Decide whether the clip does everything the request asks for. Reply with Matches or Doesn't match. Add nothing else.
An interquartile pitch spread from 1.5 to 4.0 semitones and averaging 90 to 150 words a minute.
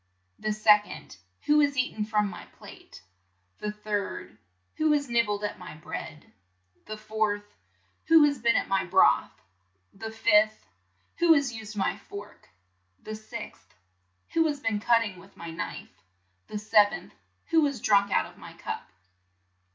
Doesn't match